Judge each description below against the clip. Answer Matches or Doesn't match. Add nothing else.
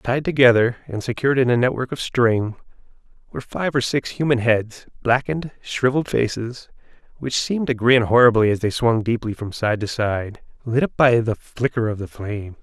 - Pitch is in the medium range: Doesn't match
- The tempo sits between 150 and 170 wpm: Doesn't match